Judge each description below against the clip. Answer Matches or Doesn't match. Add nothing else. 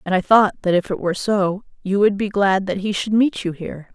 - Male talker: Doesn't match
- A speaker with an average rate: Doesn't match